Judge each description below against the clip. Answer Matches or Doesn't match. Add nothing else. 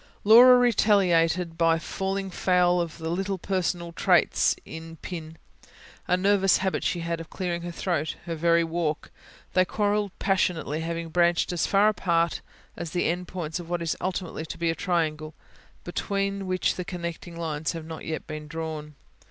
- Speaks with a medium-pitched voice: Matches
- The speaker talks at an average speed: Matches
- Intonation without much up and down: Matches